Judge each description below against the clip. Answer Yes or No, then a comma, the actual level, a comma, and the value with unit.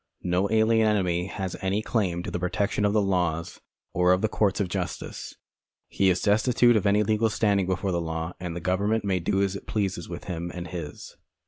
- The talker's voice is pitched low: Yes, very low, 95 Hz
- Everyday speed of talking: No, fast, 210 wpm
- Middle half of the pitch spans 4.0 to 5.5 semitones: No, average, 2.9 semitones